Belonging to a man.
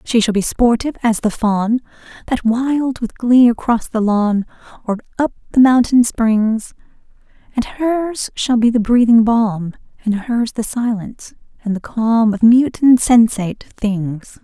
No: female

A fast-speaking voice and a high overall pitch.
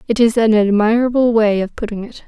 Yes: fast, 210 wpm; high, 220 Hz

